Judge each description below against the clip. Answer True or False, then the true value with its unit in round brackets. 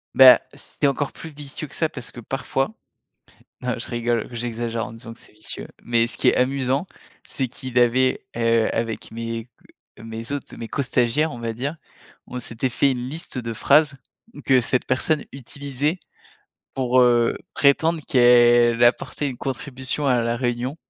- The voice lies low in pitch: True (125 Hz)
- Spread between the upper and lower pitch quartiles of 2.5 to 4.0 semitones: True (2.8 semitones)